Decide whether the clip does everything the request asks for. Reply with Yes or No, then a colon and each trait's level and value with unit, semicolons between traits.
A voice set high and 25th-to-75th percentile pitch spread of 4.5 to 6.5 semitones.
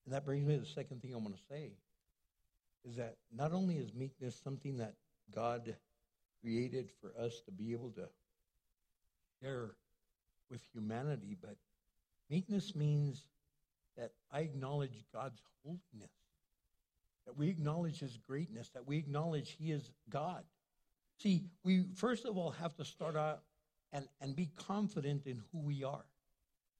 No: low, 135 Hz; average, 5.1 semitones